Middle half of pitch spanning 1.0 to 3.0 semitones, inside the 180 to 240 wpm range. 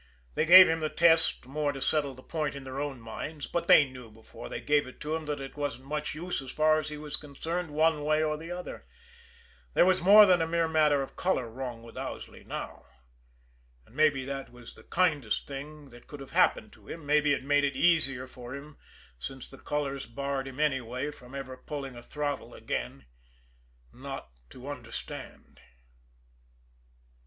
Yes: average, 2.7 semitones; average, 190 wpm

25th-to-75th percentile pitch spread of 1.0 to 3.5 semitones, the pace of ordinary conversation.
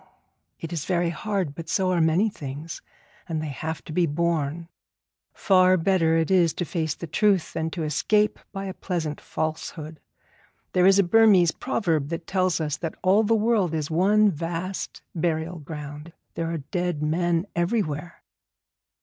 Yes: average, 2.9 semitones; average, 165 wpm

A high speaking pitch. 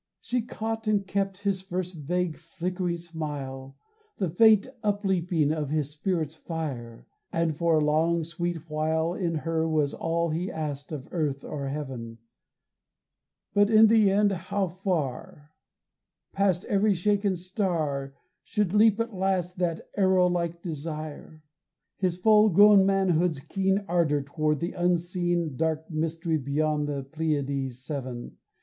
No: medium, 170 Hz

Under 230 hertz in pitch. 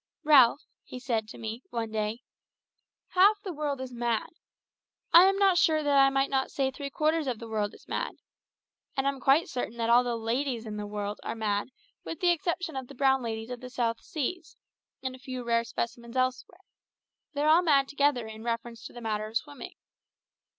No: very high, 255 Hz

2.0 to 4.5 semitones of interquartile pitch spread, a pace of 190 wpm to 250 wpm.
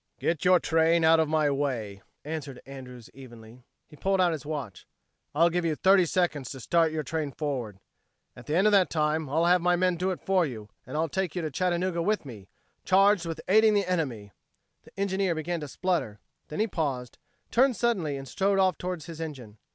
No: average, 4.9 semitones; fast, 205 wpm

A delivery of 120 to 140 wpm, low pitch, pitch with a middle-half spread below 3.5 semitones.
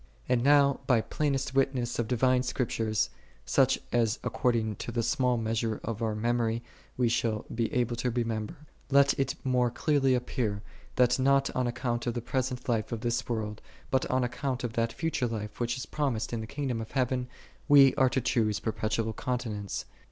No: average, 185 wpm; low, 120 Hz; narrow, 2.4 semitones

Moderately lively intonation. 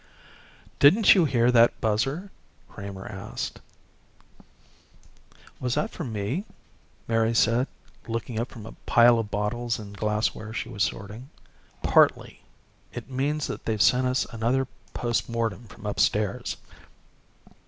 Yes: average, 3.0 semitones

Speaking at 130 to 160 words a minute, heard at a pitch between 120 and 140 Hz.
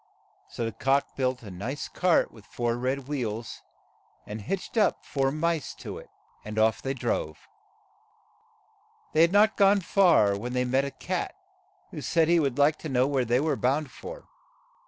No: average, 175 wpm; low, 135 Hz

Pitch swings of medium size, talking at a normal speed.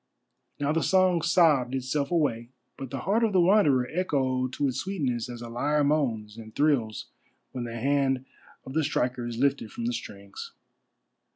Yes: average, 4.2 semitones; average, 175 wpm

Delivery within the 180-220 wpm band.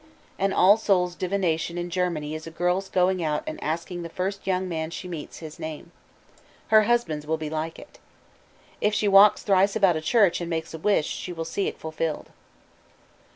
Yes: average, 195 wpm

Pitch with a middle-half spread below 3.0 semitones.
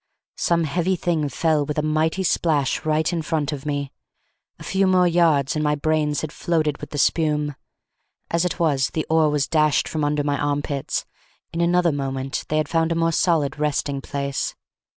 Yes: narrow, 2.4 semitones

